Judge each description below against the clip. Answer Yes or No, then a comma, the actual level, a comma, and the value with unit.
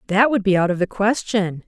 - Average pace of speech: No, fast, 250 wpm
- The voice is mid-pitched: No, high, 200 Hz